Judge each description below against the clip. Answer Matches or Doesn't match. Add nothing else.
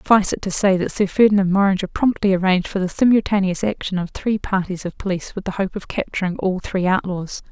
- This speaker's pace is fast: Matches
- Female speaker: Matches